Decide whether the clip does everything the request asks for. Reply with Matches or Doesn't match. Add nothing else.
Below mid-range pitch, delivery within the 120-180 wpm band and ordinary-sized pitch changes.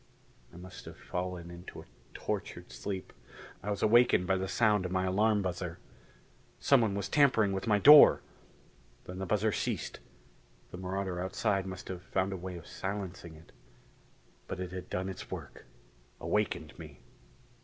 Doesn't match